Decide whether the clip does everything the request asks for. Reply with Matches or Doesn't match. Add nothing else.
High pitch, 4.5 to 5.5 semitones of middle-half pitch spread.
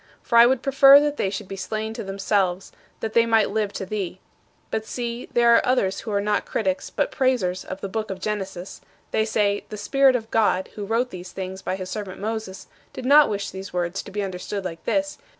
Doesn't match